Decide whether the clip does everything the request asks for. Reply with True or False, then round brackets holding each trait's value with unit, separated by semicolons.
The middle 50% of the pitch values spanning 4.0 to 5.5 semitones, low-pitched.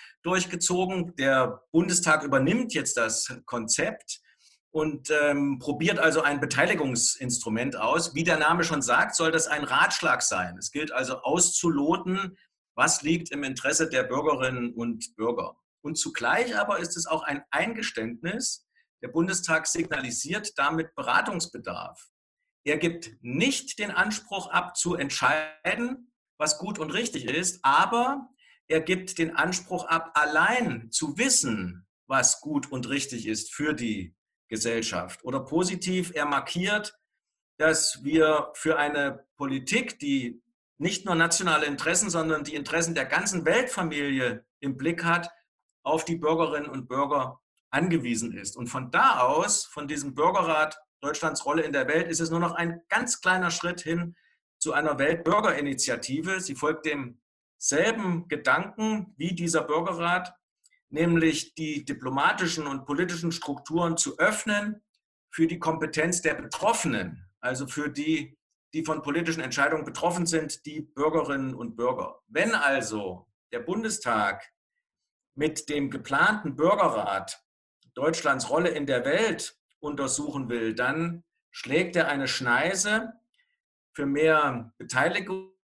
False (4.4 semitones; 160 Hz)